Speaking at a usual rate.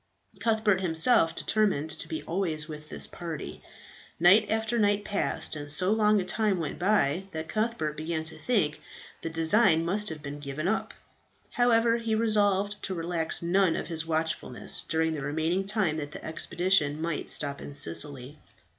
Yes: average, 165 wpm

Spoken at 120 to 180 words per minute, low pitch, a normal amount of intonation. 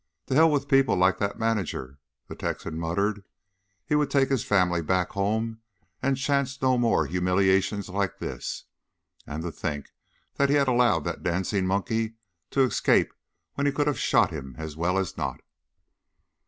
No: average, 170 wpm; low, 100 Hz; wide, 6.8 semitones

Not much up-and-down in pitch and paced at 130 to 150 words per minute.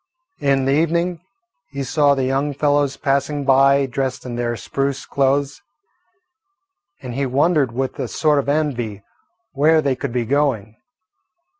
Yes: narrow, 1.8 semitones; average, 145 wpm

